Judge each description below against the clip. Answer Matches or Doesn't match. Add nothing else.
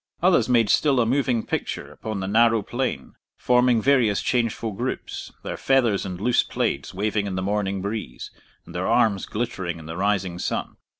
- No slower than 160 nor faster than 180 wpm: Matches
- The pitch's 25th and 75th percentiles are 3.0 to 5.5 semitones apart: Matches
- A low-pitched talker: Matches